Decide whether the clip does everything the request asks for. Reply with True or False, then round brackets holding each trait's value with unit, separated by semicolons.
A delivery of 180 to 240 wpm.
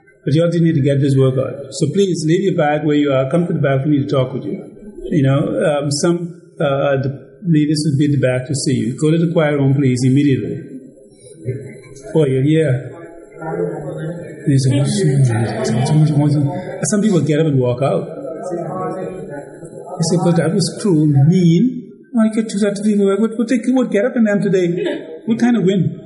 True (200 wpm)